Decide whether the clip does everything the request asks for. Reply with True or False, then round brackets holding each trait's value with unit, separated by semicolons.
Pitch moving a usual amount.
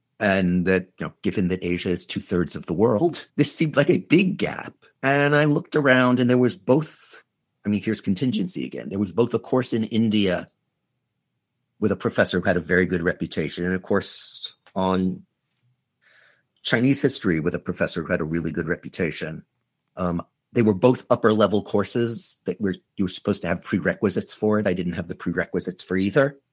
False (5.7 semitones)